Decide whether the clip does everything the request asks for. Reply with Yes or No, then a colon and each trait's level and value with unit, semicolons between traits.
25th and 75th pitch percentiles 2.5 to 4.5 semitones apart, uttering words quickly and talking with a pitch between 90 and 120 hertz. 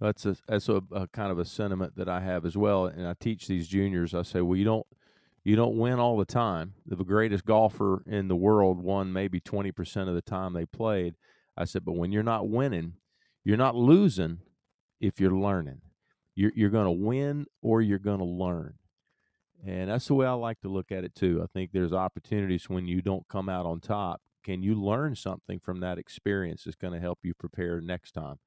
Yes: average, 2.9 semitones; fast, 220 wpm; very low, 95 Hz